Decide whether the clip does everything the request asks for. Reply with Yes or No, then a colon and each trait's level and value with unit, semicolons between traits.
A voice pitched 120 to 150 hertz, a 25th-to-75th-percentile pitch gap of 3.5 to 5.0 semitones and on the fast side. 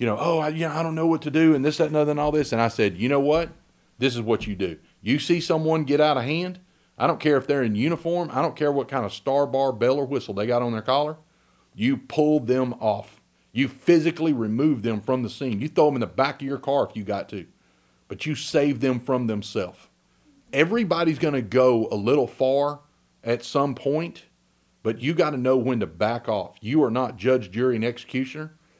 Yes: medium, 140 Hz; average, 4.2 semitones; fast, 245 wpm